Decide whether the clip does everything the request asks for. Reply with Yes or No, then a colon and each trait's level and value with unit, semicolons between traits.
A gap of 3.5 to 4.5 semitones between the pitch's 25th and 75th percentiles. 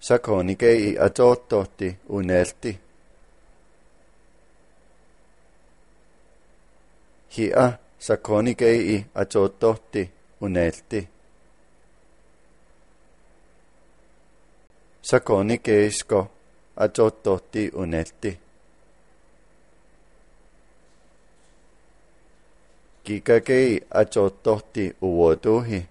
Yes: average, 4.0 semitones